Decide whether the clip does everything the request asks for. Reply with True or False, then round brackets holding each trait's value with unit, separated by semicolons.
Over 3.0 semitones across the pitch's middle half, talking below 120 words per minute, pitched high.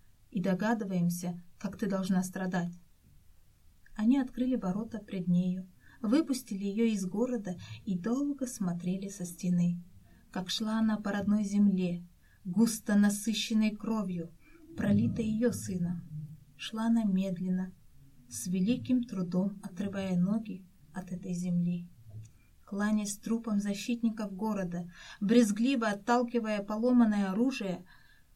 True (3.7 semitones; 110 wpm; 200 Hz)